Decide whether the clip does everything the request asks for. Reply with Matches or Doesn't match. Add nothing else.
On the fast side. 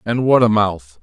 Matches